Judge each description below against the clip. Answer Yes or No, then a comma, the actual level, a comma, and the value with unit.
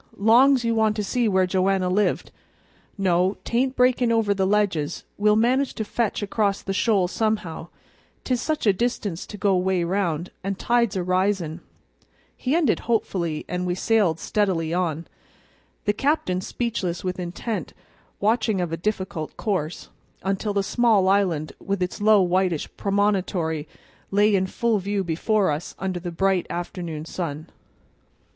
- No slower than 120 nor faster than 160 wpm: Yes, average, 150 wpm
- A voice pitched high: Yes, high, 195 Hz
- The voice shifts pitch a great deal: No, average, 3.2 semitones